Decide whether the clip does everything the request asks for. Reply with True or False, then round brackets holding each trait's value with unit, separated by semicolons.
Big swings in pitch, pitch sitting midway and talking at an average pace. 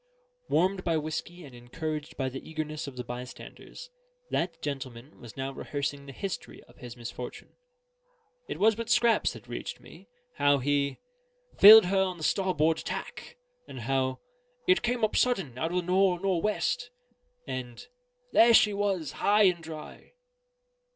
True (6.3 semitones; 160 Hz; 150 wpm)